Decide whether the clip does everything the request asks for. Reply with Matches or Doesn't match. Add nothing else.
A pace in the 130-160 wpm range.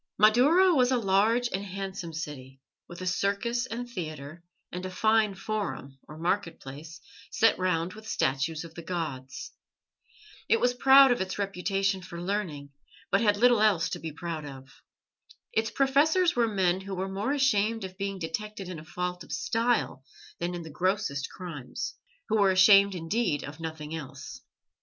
Doesn't match